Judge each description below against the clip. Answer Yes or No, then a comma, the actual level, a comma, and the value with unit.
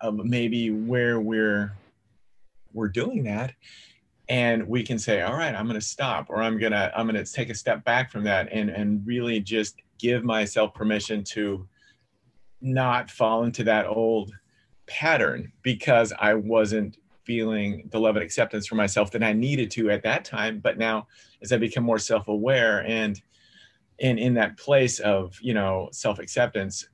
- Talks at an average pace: Yes, average, 165 wpm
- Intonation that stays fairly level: Yes, narrow, 2.0 semitones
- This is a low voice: Yes, low, 110 Hz